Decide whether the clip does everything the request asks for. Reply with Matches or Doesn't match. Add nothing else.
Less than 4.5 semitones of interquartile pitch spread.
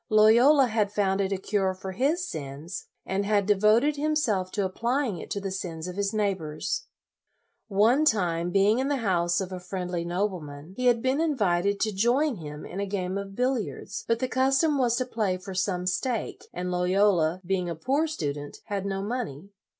Doesn't match